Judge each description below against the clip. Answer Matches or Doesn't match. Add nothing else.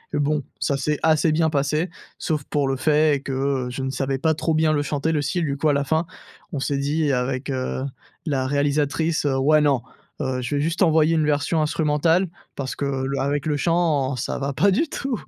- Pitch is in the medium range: Matches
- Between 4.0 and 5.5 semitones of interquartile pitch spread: Doesn't match